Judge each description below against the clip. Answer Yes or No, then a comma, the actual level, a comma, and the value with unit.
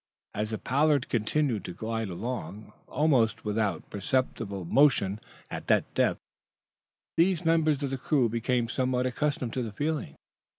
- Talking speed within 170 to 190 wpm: No, average, 140 wpm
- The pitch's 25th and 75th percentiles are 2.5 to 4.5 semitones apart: No, average, 4.9 semitones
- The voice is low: Yes, low, 125 Hz